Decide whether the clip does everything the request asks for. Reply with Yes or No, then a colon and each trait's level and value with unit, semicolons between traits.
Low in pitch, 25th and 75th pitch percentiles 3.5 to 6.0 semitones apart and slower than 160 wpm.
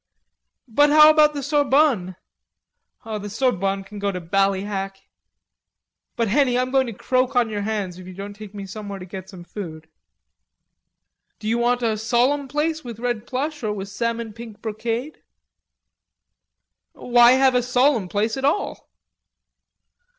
No: high, 225 Hz; average, 4.5 semitones; average, 150 wpm